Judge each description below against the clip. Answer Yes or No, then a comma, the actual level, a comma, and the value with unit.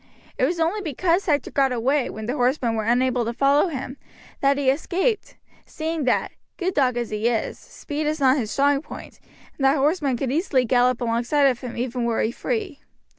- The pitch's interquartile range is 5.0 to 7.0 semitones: No, average, 3.7 semitones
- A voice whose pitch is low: No, very high, 270 Hz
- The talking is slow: No, average, 200 wpm